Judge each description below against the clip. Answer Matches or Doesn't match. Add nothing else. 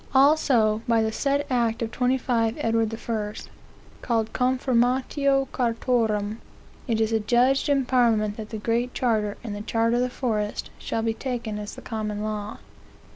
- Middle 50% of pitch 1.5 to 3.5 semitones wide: Matches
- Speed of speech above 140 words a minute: Matches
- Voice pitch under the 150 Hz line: Doesn't match